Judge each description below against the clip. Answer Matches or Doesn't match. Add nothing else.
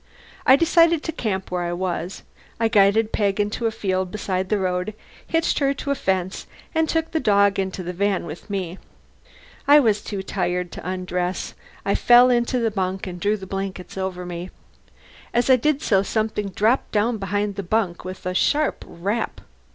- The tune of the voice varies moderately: Matches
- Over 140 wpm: Matches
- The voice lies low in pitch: Doesn't match